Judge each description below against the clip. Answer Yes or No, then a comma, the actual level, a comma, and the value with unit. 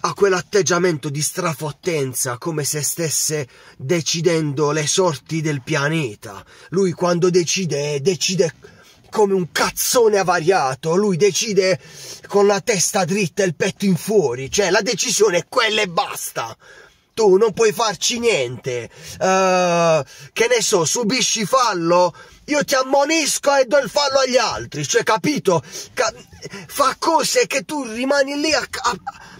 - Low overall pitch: No, medium, 185 Hz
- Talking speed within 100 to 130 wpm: No, average, 140 wpm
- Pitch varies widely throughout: Yes, wide, 6.3 semitones